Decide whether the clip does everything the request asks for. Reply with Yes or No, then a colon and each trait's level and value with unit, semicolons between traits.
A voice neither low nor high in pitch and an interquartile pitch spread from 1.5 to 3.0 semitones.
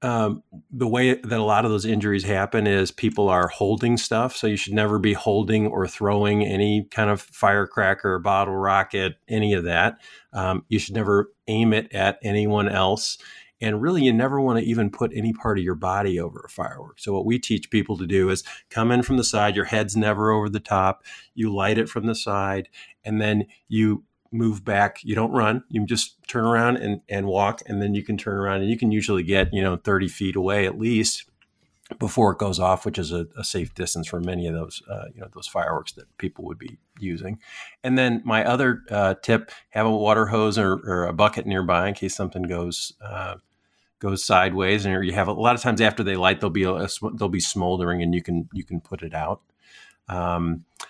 No: low, 105 Hz; narrow, 2.5 semitones